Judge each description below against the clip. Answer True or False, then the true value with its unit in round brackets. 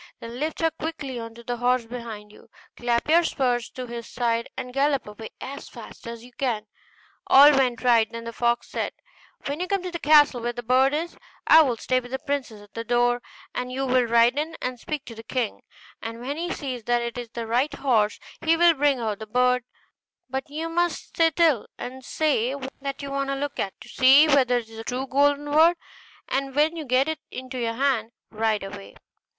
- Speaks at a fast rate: True (225 wpm)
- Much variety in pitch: False (3.4 semitones)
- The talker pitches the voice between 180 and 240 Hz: False (255 Hz)